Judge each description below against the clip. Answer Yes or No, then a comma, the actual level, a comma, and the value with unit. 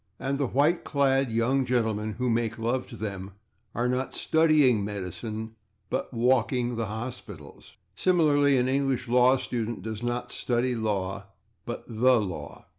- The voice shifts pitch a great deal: No, average, 3.0 semitones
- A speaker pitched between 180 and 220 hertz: No, low, 120 Hz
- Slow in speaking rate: No, average, 145 wpm